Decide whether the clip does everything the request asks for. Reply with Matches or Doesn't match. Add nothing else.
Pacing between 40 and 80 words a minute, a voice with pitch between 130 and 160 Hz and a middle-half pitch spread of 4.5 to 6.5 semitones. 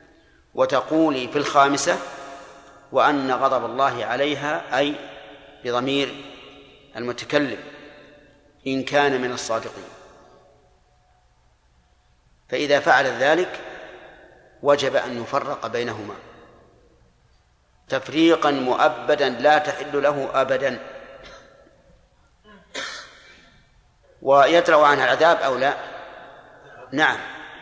Doesn't match